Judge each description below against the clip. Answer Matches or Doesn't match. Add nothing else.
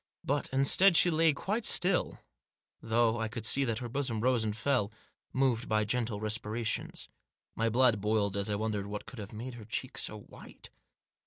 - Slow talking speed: Doesn't match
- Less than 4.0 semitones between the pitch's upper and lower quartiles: Matches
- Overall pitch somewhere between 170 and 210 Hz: Doesn't match